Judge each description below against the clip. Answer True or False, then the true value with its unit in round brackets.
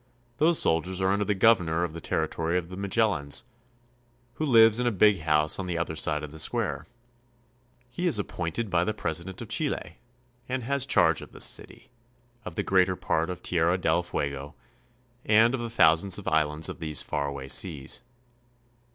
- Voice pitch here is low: True (90 Hz)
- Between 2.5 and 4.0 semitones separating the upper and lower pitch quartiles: False (5.2 semitones)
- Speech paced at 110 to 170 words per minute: False (185 wpm)